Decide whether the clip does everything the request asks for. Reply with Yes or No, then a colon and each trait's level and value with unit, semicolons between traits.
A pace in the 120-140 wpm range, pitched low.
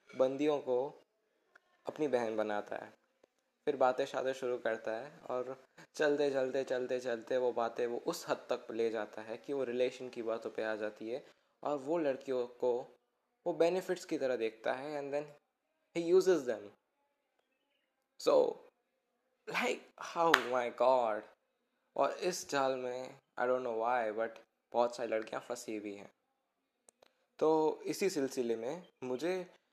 No: average, 150 wpm; low, 130 Hz